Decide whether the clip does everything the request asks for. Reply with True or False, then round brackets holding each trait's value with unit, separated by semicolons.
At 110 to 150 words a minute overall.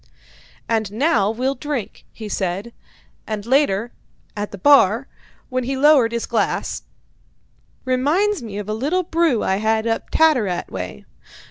True (140 wpm)